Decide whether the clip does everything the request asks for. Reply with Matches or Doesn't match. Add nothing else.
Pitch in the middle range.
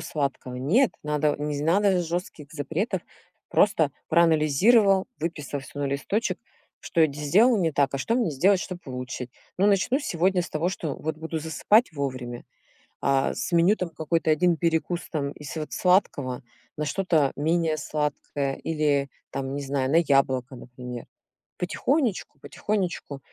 Matches